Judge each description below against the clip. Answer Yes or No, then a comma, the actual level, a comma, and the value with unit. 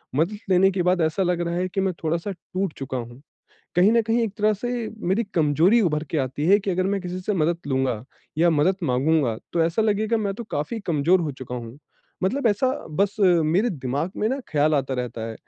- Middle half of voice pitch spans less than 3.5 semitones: No, average, 5.2 semitones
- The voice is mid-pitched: Yes, medium, 175 Hz